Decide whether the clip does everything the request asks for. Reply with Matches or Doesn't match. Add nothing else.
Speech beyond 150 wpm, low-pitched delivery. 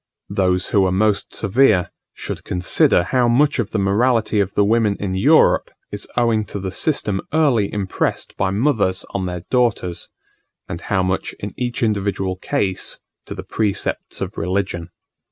Matches